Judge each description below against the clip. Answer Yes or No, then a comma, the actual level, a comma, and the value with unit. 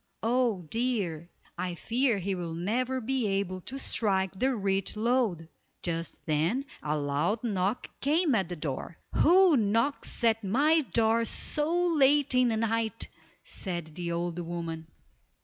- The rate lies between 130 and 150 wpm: Yes, average, 145 wpm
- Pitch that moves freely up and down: Yes, wide, 6.5 semitones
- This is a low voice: No, high, 215 Hz